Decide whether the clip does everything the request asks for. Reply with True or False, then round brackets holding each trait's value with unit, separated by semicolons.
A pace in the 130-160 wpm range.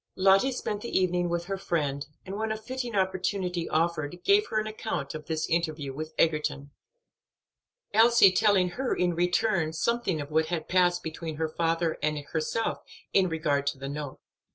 False (175 wpm)